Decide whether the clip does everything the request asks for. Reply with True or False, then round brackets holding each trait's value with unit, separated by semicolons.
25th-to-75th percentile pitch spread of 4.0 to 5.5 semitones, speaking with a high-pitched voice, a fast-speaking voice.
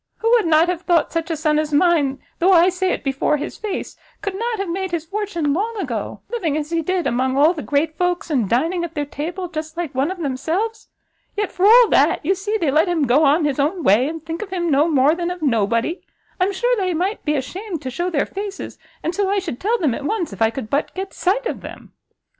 True (4.5 semitones; 335 Hz; 250 wpm)